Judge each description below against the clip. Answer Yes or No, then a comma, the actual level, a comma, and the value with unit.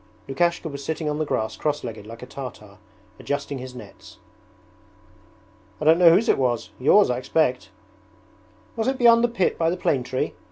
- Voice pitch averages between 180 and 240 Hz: No, medium, 145 Hz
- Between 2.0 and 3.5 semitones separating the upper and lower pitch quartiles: No, wide, 5.4 semitones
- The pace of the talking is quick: No, average, 175 wpm